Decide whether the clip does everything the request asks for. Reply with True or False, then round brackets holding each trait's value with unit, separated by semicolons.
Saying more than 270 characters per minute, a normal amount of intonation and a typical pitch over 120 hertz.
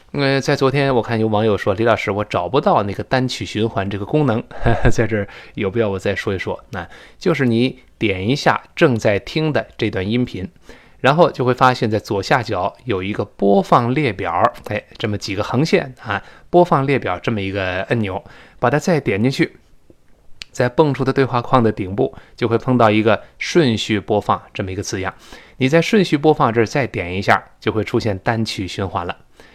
False (290 characters per minute; 4.5 semitones; 115 Hz)